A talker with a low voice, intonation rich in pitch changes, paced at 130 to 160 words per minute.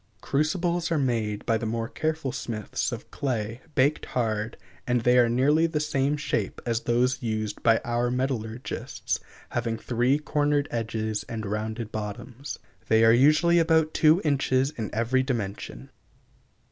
No: low, 125 Hz; average, 4.3 semitones; average, 145 wpm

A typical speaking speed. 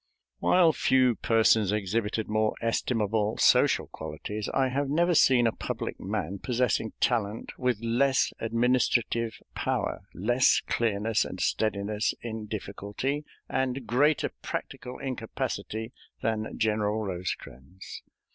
No: slow, 110 wpm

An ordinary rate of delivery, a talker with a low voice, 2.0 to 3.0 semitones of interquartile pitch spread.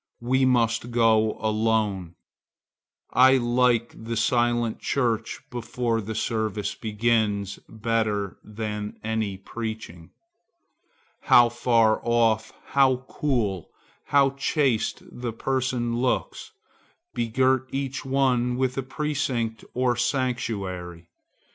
No: slow, 95 wpm; low, 115 Hz; narrow, 2.6 semitones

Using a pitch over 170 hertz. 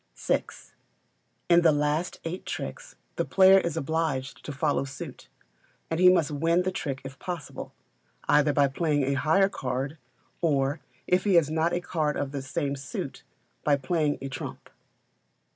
No: medium, 150 Hz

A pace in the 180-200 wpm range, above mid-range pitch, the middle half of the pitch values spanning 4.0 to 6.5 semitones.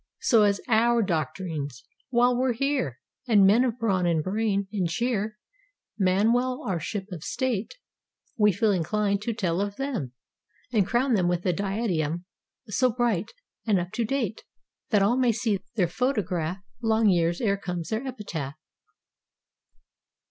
No: average, 150 wpm; high, 205 Hz; average, 4.8 semitones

